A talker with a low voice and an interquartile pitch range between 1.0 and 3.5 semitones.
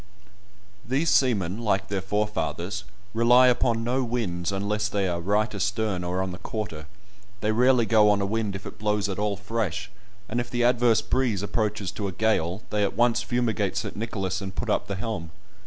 Yes: low, 105 Hz; average, 3.0 semitones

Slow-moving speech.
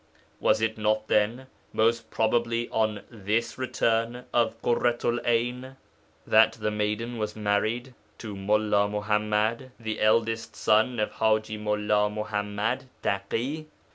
Yes: slow, 120 wpm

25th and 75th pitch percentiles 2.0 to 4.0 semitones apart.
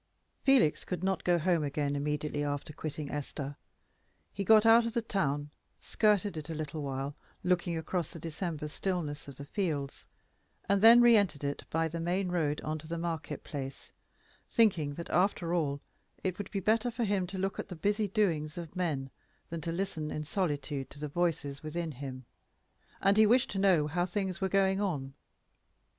No: average, 4.8 semitones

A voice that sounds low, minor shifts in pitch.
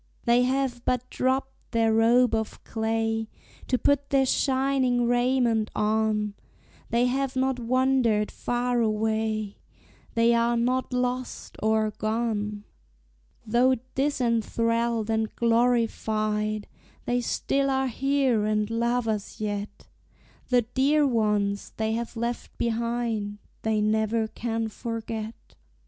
No: high, 230 Hz; narrow, 2.3 semitones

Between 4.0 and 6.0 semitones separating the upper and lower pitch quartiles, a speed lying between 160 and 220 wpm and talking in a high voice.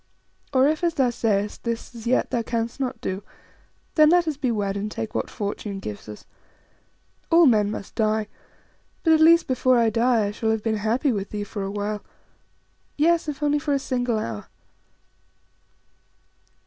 Yes: average, 5.0 semitones; average, 180 wpm; high, 230 Hz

